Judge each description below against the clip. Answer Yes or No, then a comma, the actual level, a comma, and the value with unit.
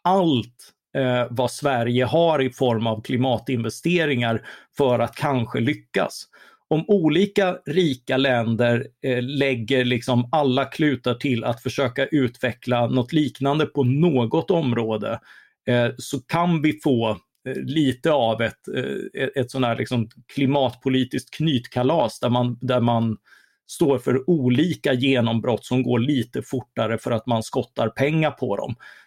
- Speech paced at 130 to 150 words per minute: Yes, average, 135 wpm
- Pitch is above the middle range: No, low, 130 Hz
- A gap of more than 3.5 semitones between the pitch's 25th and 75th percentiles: No, average, 3.0 semitones